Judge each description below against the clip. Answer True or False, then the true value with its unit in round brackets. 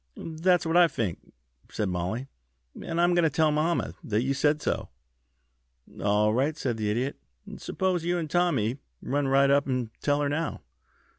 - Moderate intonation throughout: False (5.7 semitones)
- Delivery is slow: False (170 wpm)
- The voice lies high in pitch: False (145 Hz)